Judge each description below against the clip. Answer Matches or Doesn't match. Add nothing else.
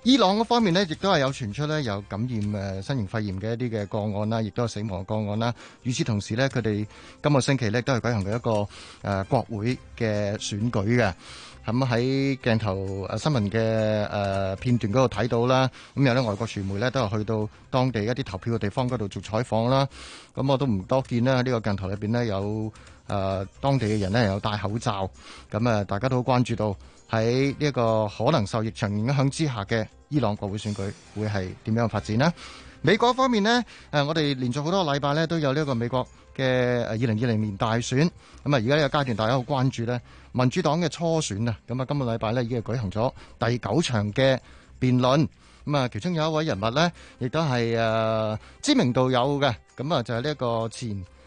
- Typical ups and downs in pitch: Matches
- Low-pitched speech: Matches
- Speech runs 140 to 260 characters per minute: Doesn't match